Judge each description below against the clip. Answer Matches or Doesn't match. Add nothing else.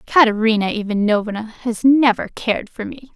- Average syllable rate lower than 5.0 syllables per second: Doesn't match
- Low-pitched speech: Doesn't match